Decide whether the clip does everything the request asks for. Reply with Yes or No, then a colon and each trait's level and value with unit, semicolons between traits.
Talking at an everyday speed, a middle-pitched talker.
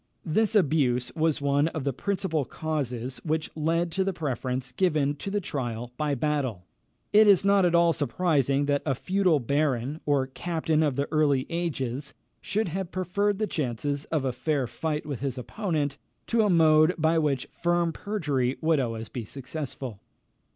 Yes: average, 170 wpm; medium, 150 Hz